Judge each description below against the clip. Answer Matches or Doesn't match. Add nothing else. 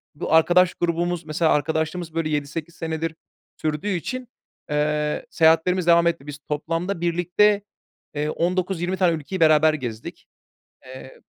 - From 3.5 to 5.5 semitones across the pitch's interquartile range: Doesn't match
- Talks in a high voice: Doesn't match